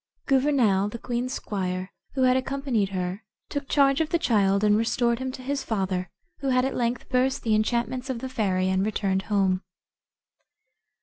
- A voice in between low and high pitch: No, high, 235 Hz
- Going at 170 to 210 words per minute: Yes, average, 175 wpm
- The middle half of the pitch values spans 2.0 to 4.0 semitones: No, average, 4.9 semitones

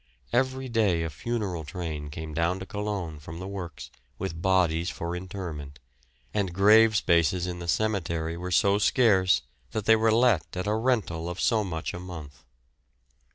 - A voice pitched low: Yes, very low, 90 Hz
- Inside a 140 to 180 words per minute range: Yes, average, 165 wpm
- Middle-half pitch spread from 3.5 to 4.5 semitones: Yes, average, 4.1 semitones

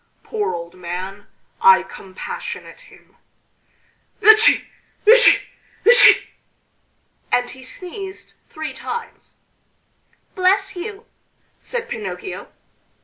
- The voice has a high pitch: Yes, very high, 385 Hz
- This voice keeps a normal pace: No, slow, 85 wpm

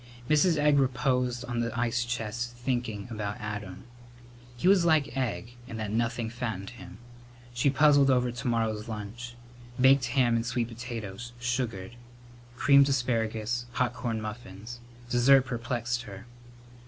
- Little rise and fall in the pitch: Yes, narrow, 2.2 semitones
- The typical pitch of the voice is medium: No, low, 120 Hz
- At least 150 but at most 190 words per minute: No, average, 140 wpm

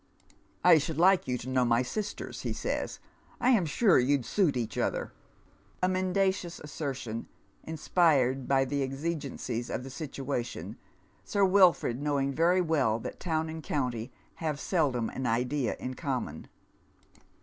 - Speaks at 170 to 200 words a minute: No, average, 155 wpm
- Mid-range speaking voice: Yes, medium, 145 Hz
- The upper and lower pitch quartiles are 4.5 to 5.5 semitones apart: Yes, average, 5.1 semitones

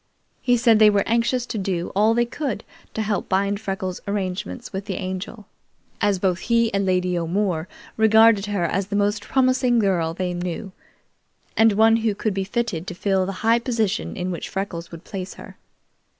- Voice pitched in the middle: No, high, 200 Hz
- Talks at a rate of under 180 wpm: No, average, 185 wpm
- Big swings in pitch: No, average, 3.2 semitones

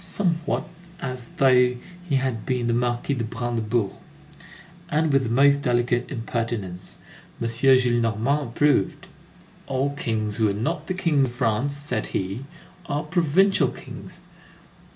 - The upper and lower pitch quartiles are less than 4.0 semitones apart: Yes, average, 3.6 semitones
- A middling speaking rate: No, slow, 130 wpm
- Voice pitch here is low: Yes, low, 125 Hz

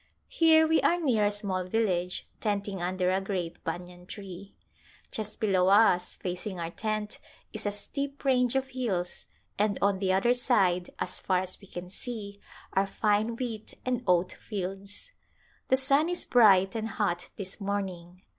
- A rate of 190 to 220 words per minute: No, average, 165 wpm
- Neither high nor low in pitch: No, high, 200 Hz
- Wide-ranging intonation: No, average, 3.7 semitones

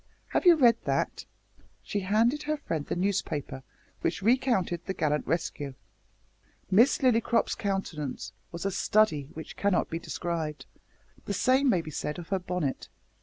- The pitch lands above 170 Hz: Yes, medium, 185 Hz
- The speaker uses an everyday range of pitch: No, wide, 6.4 semitones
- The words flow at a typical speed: Yes, average, 150 wpm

